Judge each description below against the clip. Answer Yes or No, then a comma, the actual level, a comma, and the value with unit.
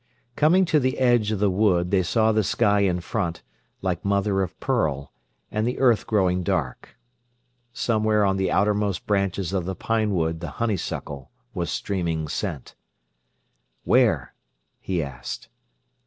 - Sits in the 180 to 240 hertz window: No, low, 100 Hz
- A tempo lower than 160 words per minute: Yes, average, 145 wpm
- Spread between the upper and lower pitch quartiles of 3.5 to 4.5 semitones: Yes, average, 3.8 semitones